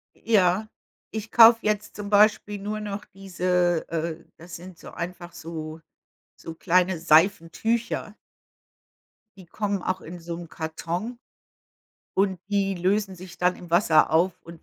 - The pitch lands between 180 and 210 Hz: Yes, medium, 185 Hz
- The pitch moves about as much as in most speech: Yes, average, 3.3 semitones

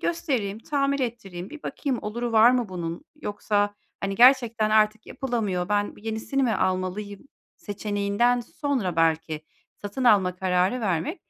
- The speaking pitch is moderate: No, high, 210 Hz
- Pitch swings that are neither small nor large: Yes, average, 4.2 semitones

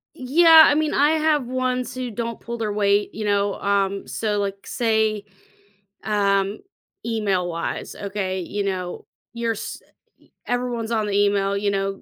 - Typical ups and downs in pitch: Yes, average, 3.4 semitones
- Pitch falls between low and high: No, high, 210 Hz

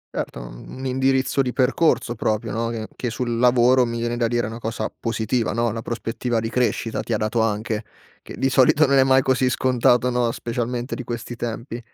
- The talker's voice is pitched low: Yes, low, 120 Hz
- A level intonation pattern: Yes, narrow, 1.9 semitones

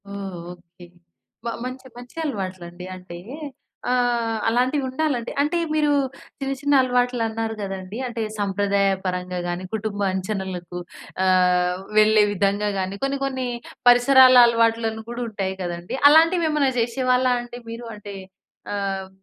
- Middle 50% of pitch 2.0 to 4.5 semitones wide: No, average, 4.9 semitones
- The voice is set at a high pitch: Yes, high, 220 Hz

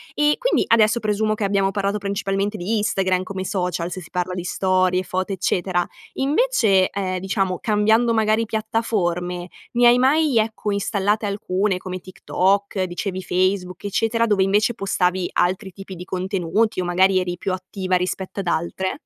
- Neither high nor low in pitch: No, high, 195 Hz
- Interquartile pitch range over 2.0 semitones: Yes, narrow, 2.6 semitones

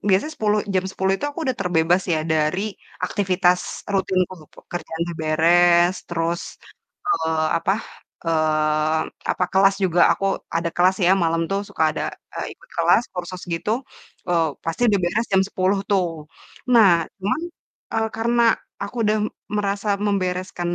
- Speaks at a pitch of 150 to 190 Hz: Yes, medium, 185 Hz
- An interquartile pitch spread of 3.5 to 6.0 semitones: No, average, 3.1 semitones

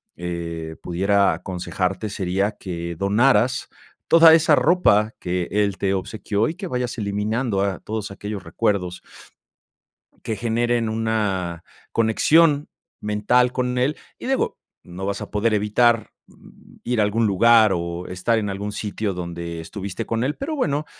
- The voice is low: Yes, low, 105 Hz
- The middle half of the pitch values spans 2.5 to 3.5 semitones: No, average, 3.9 semitones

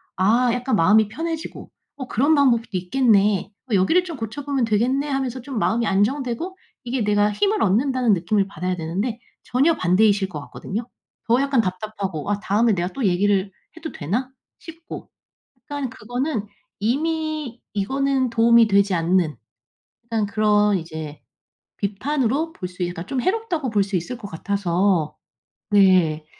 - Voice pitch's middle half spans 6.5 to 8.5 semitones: No, wide, 5.4 semitones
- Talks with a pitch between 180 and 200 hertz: No, high, 220 Hz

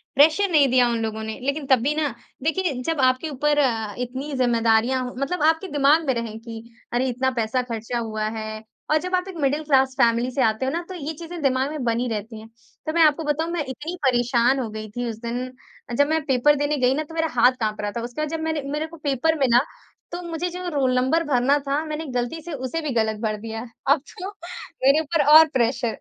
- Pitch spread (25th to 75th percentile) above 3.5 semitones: Yes, average, 4.6 semitones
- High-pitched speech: Yes, very high, 265 Hz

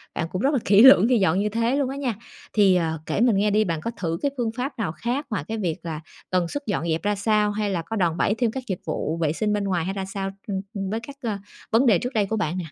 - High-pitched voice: Yes, high, 205 Hz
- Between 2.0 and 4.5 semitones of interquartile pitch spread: Yes, average, 4.2 semitones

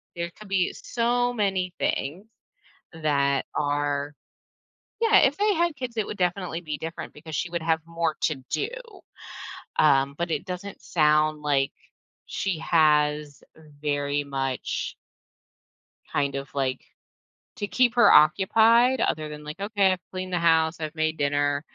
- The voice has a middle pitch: Yes, medium, 160 Hz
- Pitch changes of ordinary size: Yes, average, 5.0 semitones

